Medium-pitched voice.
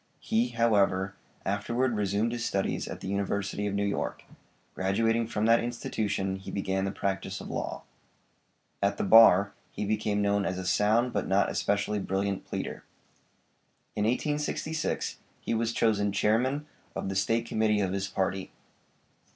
No: low, 105 Hz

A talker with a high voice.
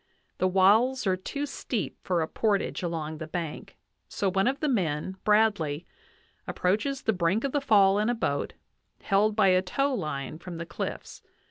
Yes: high, 195 Hz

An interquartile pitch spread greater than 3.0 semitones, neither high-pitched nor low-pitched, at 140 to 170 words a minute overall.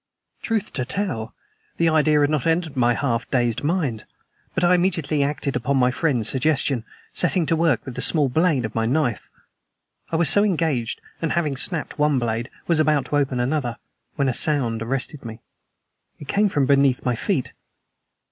No: average, 4.7 semitones; medium, 145 Hz; average, 180 wpm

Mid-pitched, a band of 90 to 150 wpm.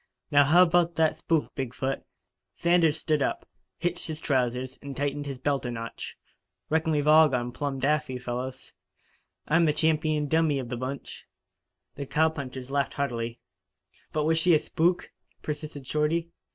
No: medium, 145 Hz; average, 160 wpm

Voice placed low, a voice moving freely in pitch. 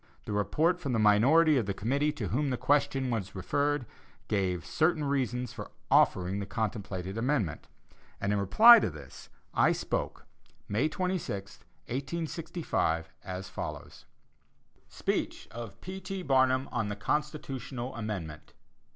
Yes: low, 125 Hz; wide, 6.7 semitones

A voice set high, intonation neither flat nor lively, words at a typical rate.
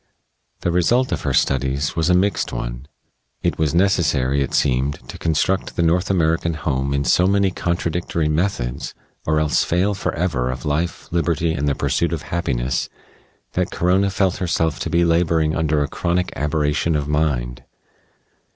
No: very low, 80 Hz; average, 3.6 semitones; average, 160 wpm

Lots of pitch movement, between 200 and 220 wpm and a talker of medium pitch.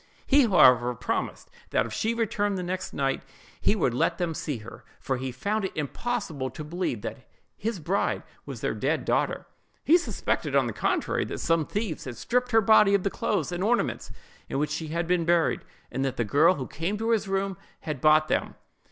Yes: wide, 6.4 semitones; fast, 205 wpm; medium, 175 Hz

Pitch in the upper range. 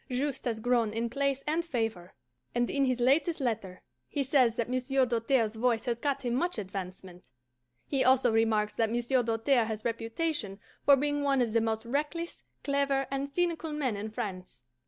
Yes: high, 245 Hz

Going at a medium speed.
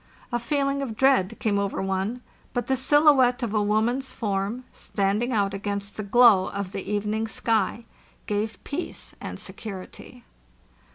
Yes: average, 150 wpm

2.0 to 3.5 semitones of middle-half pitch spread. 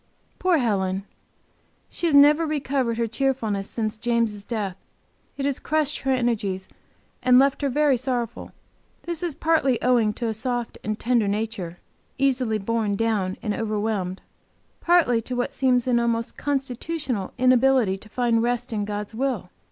No: average, 3.9 semitones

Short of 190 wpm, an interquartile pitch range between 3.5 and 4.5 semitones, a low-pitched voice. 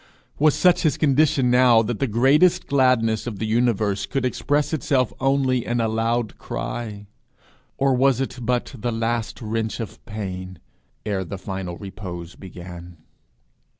Yes: average, 150 wpm; average, 4.2 semitones; low, 115 Hz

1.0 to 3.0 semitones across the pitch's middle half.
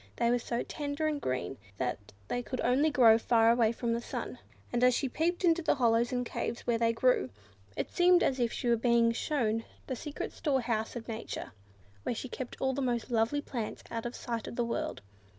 Yes: narrow, 2.6 semitones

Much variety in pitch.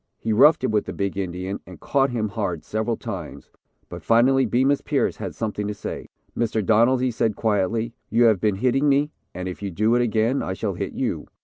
No: average, 3.3 semitones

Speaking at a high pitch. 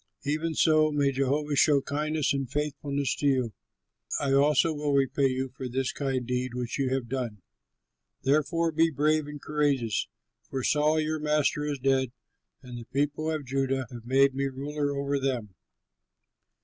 No: medium, 140 Hz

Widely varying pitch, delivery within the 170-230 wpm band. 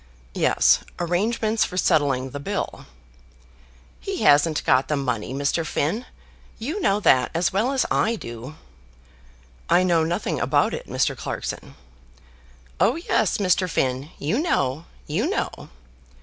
No: wide, 7.1 semitones; slow, 135 wpm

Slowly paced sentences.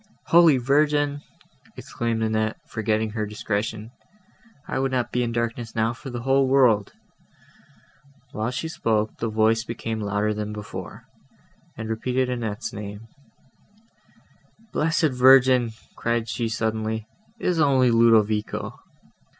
Yes: slow, 125 wpm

